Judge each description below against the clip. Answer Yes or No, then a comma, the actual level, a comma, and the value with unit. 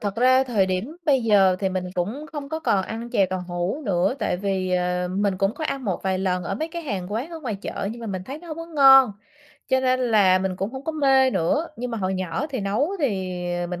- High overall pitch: Yes, high, 210 Hz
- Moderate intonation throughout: No, wide, 6.2 semitones